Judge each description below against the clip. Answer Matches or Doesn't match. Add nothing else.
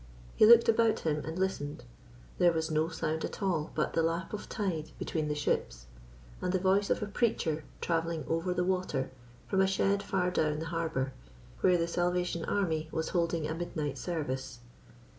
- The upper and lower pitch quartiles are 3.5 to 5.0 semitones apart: Doesn't match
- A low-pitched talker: Doesn't match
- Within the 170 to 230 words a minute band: Matches